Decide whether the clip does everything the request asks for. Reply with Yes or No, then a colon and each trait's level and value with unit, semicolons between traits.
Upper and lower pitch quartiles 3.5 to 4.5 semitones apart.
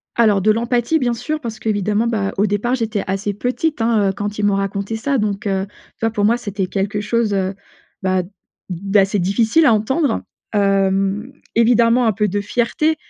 No: average, 2.9 semitones